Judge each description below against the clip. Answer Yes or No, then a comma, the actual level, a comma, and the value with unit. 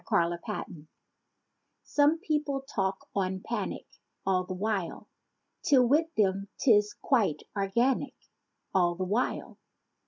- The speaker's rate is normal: No, slow, 120 wpm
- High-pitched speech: Yes, high, 205 Hz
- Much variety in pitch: Yes, wide, 6.1 semitones